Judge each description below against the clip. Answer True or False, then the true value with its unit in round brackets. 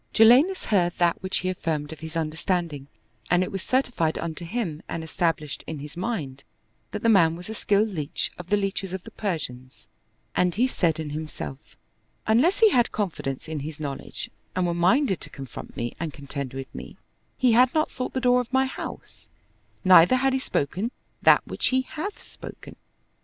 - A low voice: False (175 Hz)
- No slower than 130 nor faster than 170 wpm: False (190 wpm)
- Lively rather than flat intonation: True (6.8 semitones)